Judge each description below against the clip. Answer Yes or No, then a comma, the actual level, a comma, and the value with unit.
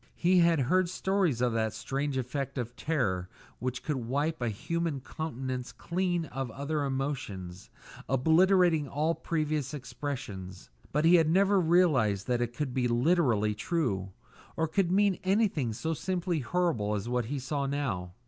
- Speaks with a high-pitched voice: No, medium, 140 Hz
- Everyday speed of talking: Yes, average, 155 wpm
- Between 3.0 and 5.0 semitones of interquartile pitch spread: No, wide, 5.6 semitones